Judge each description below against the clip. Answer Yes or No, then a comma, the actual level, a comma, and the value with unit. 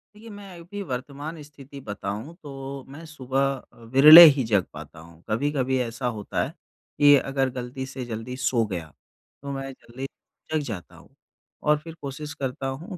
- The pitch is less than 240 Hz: Yes, low, 135 Hz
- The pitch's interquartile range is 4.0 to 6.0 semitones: No, average, 3.3 semitones